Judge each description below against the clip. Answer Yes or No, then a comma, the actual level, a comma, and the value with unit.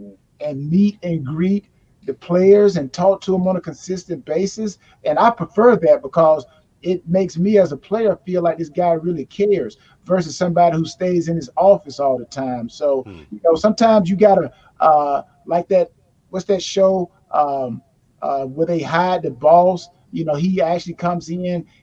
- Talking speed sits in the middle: Yes, average, 185 wpm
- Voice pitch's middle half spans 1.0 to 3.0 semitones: No, average, 3.9 semitones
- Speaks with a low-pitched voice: No, medium, 175 Hz